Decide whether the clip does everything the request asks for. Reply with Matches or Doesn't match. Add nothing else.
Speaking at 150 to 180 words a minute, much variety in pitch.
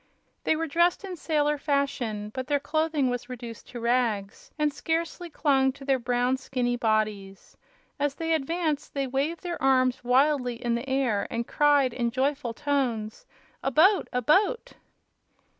Doesn't match